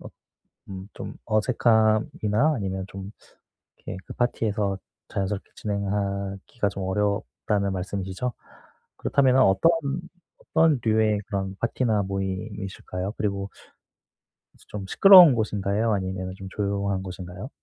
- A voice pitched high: No, low, 100 Hz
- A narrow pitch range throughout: Yes, narrow, 2.3 semitones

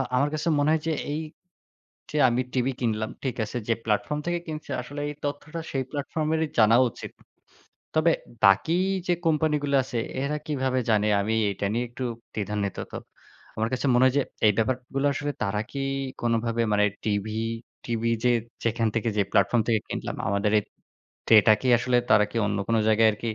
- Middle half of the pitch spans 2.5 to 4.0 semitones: No, average, 4.9 semitones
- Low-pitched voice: Yes, low, 120 Hz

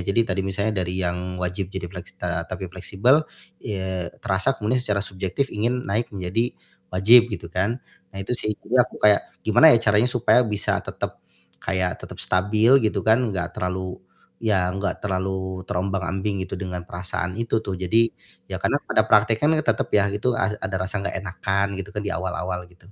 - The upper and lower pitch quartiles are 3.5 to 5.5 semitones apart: No, average, 3.0 semitones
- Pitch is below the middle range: Yes, very low, 95 Hz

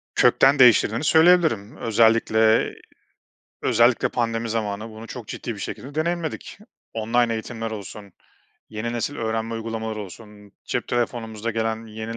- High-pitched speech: No, low, 115 Hz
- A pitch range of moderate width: No, narrow, 1.5 semitones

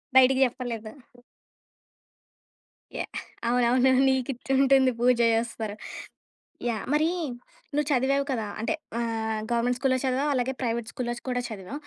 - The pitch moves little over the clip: Yes, narrow, 2.2 semitones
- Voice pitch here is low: No, very high, 250 Hz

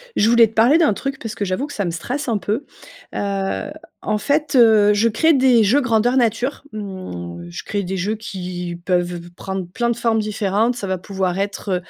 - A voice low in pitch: No, high, 210 Hz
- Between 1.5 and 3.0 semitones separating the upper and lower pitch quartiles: No, average, 4.0 semitones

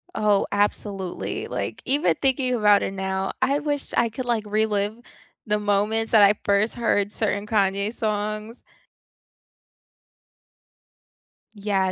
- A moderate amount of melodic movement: No, narrow, 2.0 semitones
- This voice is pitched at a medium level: No, high, 210 Hz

